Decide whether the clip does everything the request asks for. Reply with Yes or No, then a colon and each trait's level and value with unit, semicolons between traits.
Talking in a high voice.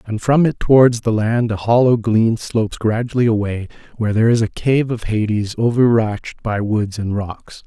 No: low, 115 Hz